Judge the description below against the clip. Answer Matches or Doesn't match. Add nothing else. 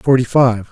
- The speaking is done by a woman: Doesn't match